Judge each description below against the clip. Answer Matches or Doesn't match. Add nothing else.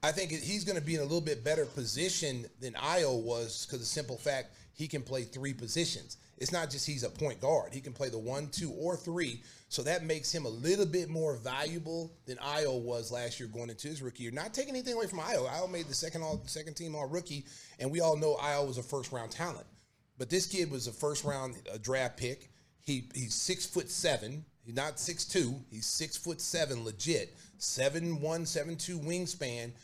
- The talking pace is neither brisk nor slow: Doesn't match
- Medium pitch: Matches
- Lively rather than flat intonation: Doesn't match